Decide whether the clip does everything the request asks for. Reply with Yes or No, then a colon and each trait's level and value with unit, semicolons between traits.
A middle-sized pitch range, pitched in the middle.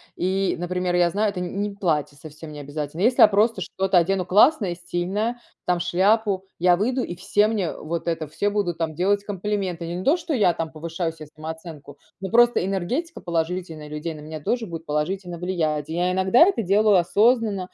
Yes: average, 3.8 semitones; medium, 180 Hz